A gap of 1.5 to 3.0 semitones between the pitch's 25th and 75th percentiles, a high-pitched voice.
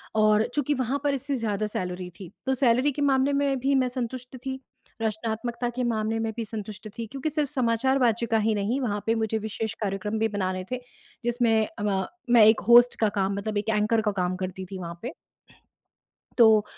No: average, 3.4 semitones; high, 225 Hz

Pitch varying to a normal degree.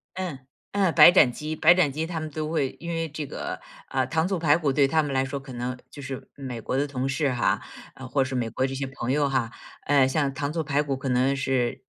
Yes: average, 3.0 semitones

